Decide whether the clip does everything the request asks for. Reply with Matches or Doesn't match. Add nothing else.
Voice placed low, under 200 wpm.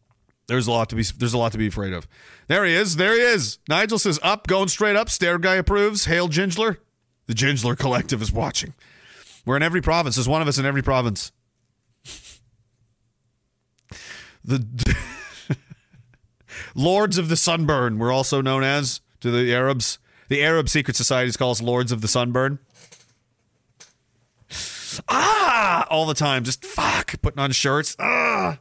Matches